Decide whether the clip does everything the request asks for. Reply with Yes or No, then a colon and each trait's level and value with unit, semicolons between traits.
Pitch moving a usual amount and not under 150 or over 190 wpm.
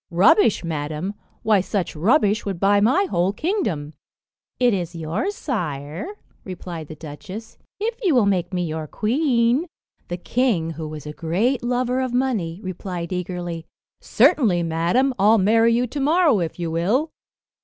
No: wide, 6.8 semitones; average, 155 wpm